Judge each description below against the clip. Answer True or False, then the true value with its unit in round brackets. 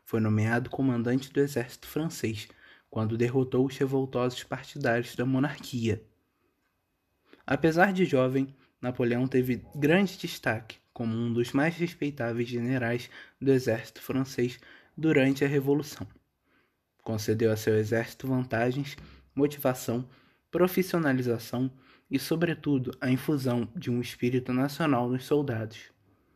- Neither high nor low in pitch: False (130 Hz)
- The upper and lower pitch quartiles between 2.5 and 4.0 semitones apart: True (3.1 semitones)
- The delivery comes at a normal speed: False (110 wpm)